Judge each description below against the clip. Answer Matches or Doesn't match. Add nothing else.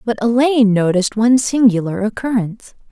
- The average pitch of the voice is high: Matches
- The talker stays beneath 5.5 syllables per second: Doesn't match